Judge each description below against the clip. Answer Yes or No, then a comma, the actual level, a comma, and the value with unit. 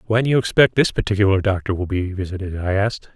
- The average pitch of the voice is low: Yes, low, 100 Hz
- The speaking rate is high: Yes, fast, 230 wpm